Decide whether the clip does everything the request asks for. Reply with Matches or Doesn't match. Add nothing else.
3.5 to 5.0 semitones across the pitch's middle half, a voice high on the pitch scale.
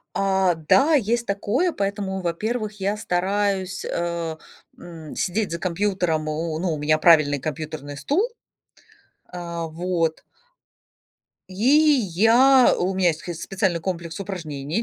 Doesn't match